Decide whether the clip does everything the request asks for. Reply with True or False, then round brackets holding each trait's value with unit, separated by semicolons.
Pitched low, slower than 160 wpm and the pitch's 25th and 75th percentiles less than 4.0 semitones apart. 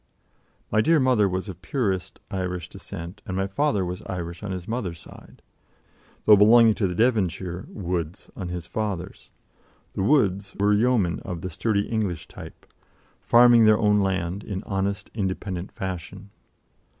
True (95 Hz; 150 wpm; 3.0 semitones)